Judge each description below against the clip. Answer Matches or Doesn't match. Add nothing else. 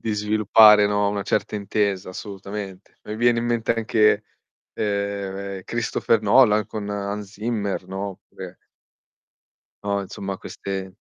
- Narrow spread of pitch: Matches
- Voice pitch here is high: Doesn't match